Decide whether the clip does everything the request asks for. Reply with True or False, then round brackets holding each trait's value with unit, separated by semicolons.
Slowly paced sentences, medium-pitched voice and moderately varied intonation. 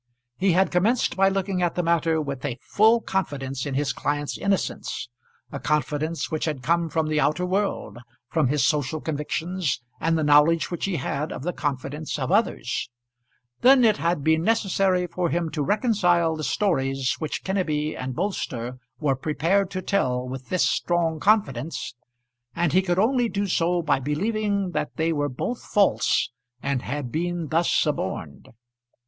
False (165 wpm; 165 Hz; 4.5 semitones)